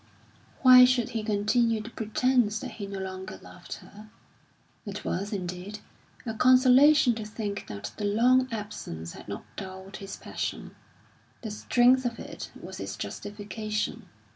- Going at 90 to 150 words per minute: Yes, average, 145 wpm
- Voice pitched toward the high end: Yes, high, 215 Hz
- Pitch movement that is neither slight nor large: Yes, average, 3.4 semitones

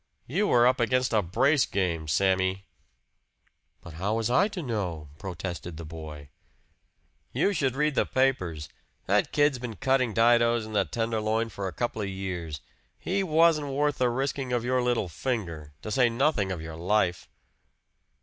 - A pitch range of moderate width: No, wide, 6.0 semitones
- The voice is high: No, low, 115 Hz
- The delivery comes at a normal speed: Yes, average, 165 wpm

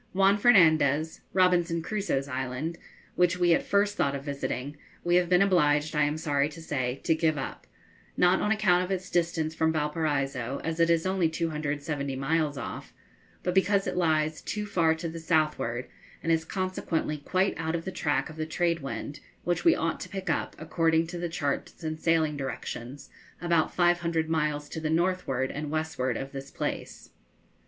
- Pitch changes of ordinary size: Yes, average, 3.1 semitones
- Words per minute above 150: Yes, average, 180 wpm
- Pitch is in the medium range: Yes, medium, 160 Hz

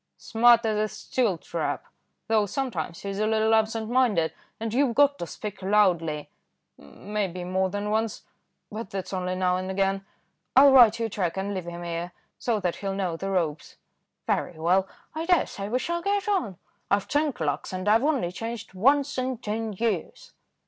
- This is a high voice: Yes, high, 210 Hz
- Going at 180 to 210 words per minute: Yes, average, 185 wpm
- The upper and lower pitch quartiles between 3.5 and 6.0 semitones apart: Yes, average, 4.1 semitones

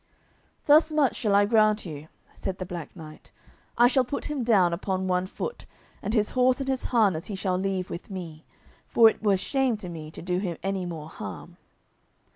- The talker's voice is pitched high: Yes, high, 195 Hz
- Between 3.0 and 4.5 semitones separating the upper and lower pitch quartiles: No, average, 4.9 semitones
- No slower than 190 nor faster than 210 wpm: Yes, average, 200 wpm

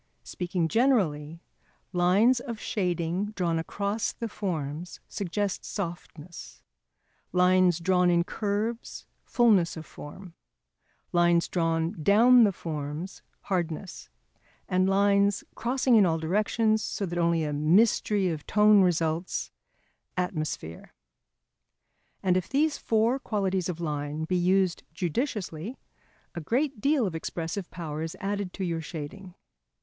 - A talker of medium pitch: Yes, medium, 180 Hz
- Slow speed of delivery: Yes, slow, 120 wpm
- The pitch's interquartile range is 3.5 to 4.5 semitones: Yes, average, 3.8 semitones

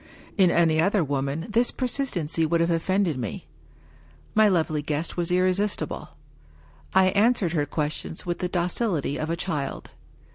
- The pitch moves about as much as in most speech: Yes, average, 3.5 semitones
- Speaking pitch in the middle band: Yes, medium, 170 Hz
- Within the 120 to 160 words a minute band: Yes, average, 145 wpm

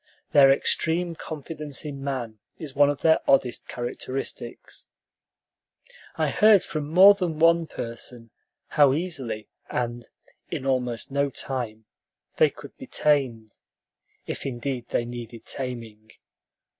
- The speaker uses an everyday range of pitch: Yes, average, 4.2 semitones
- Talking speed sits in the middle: No, slow, 120 wpm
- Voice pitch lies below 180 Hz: Yes, low, 135 Hz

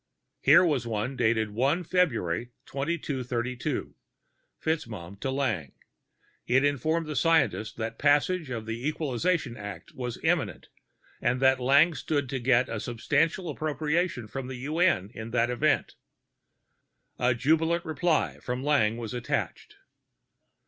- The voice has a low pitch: Yes, low, 130 Hz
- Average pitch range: Yes, average, 4.8 semitones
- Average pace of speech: No, slow, 130 wpm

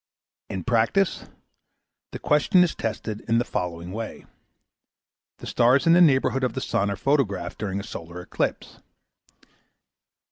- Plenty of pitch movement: Yes, wide, 5.7 semitones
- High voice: No, low, 115 Hz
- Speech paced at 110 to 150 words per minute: Yes, average, 140 wpm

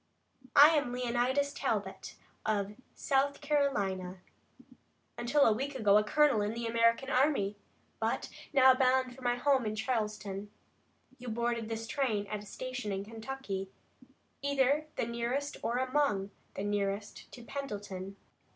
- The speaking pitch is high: Yes, high, 235 Hz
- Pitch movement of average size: Yes, average, 4.5 semitones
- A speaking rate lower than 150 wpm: Yes, average, 140 wpm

